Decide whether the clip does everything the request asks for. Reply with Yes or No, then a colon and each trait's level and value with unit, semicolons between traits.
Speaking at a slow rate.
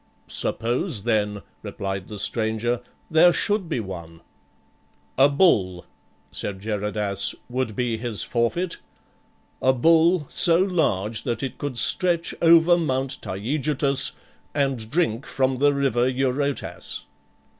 Yes: slow, 120 wpm